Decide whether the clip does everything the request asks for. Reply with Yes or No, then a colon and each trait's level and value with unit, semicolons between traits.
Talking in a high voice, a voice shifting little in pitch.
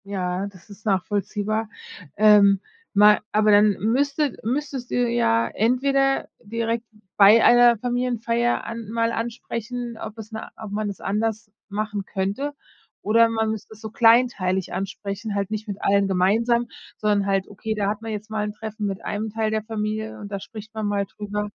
Yes: high, 215 Hz; narrow, 2.2 semitones